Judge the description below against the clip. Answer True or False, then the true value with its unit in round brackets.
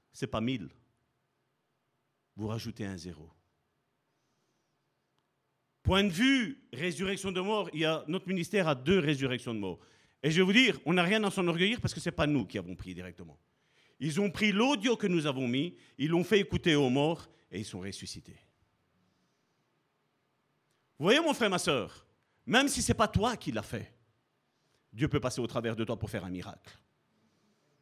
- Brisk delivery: False (190 wpm)